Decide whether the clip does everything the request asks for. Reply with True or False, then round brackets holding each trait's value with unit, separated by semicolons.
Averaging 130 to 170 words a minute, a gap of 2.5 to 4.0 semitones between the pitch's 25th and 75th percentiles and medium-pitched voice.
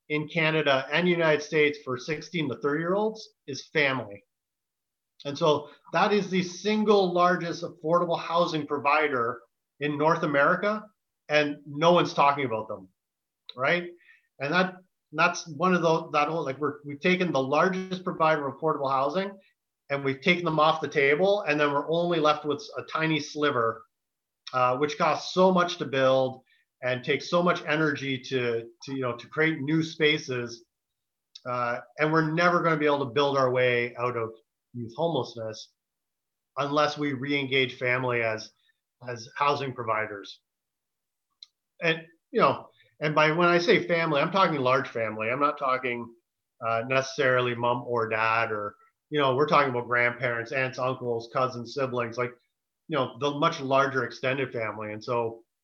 False (165 wpm; 4.8 semitones; 145 Hz)